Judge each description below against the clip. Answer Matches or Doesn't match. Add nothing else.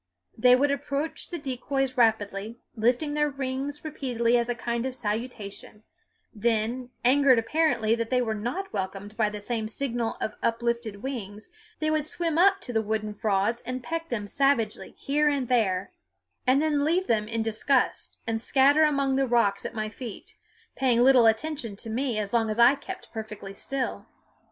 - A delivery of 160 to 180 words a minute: Matches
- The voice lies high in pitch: Matches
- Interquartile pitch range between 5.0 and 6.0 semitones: Doesn't match